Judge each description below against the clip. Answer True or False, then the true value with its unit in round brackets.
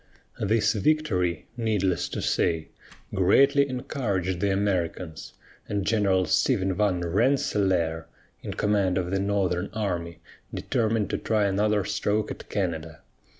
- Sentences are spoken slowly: True (120 wpm)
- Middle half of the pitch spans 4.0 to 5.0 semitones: False (3.0 semitones)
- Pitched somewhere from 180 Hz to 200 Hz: False (100 Hz)